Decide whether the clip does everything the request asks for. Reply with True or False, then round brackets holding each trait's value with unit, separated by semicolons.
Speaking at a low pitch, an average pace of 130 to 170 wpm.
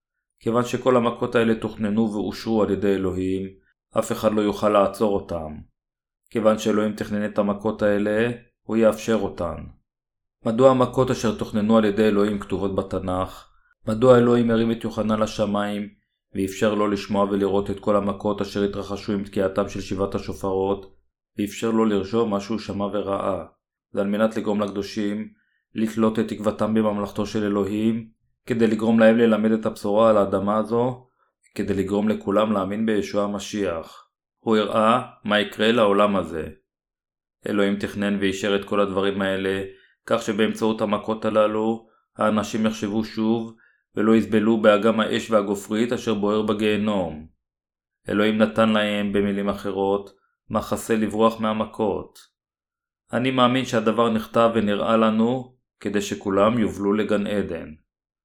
True (105 Hz; 135 wpm)